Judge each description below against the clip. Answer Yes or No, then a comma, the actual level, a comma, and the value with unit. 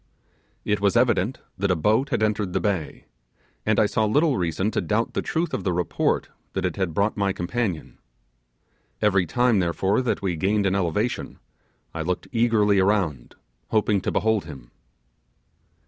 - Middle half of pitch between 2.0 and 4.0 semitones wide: Yes, average, 3.2 semitones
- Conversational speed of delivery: Yes, average, 165 wpm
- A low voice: Yes, low, 100 Hz